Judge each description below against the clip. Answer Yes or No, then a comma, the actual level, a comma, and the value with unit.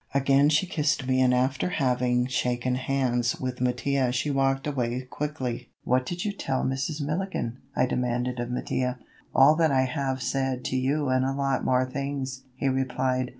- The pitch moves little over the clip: Yes, narrow, 1.6 semitones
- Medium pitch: No, low, 130 Hz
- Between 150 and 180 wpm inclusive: Yes, average, 175 wpm